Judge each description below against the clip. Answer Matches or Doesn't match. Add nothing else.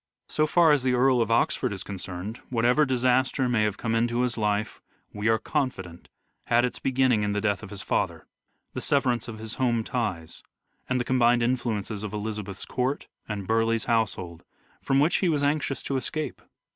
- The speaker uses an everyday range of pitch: Matches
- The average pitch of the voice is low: Matches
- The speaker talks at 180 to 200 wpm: Matches